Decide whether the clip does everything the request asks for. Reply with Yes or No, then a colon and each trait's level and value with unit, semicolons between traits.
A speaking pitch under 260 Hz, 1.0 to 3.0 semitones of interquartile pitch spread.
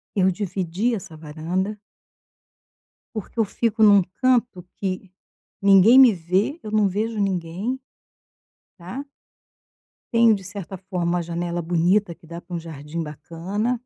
No: high, 190 Hz; average, 3.9 semitones